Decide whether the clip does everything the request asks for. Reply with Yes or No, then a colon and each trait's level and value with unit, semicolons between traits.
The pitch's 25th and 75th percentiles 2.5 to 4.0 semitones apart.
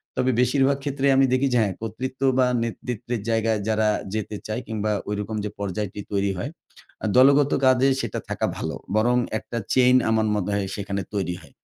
Yes: average, 3.7 semitones